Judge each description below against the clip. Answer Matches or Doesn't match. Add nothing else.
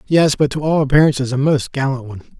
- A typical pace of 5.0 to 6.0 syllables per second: Doesn't match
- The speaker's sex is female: Doesn't match